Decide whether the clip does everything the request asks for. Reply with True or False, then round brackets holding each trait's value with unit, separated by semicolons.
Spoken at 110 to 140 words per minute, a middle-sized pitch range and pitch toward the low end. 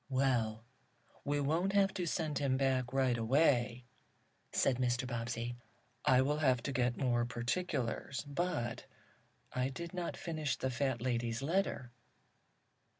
True (135 wpm; 3.3 semitones; 130 Hz)